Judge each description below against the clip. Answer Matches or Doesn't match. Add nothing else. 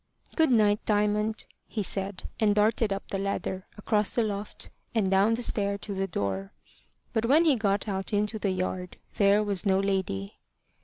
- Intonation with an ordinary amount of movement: Doesn't match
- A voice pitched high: Matches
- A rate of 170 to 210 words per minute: Matches